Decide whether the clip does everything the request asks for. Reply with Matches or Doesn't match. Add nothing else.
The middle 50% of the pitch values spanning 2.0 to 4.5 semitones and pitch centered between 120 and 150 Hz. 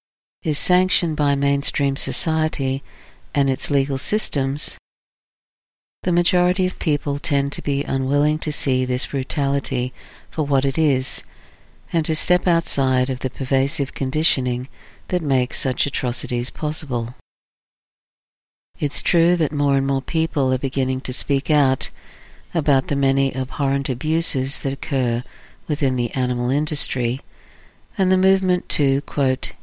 Matches